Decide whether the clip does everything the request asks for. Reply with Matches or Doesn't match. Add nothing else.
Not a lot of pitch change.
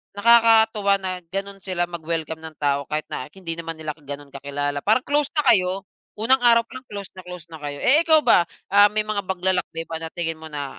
Doesn't match